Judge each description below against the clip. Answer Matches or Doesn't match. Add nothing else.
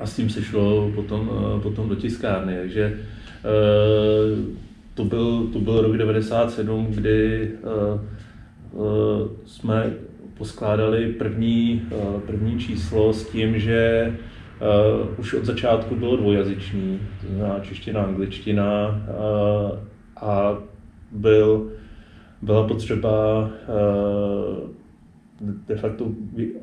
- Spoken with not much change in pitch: Matches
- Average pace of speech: Doesn't match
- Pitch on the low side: Matches